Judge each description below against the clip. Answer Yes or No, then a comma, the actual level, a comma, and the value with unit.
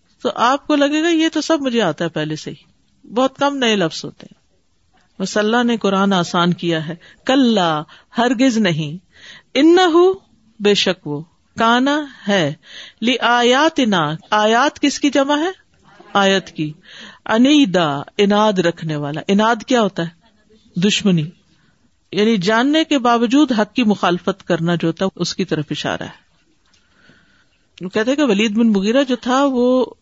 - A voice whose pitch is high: Yes, high, 215 Hz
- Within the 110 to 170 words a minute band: Yes, average, 140 wpm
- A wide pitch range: Yes, wide, 6.8 semitones